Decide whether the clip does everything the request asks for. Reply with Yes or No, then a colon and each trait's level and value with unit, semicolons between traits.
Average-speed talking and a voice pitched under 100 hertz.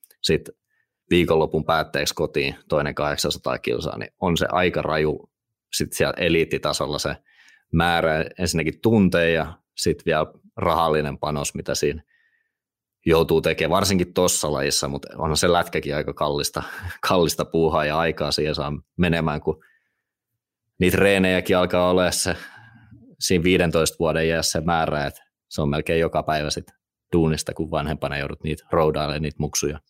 Yes: average, 140 wpm; very low, 80 Hz